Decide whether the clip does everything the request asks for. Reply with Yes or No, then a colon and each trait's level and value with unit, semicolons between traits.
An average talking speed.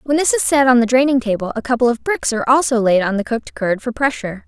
No: fast, 280 wpm